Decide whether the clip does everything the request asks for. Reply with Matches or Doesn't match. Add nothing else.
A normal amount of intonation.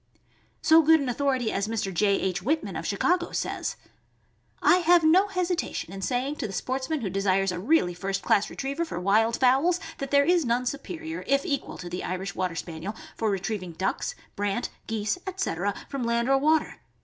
Doesn't match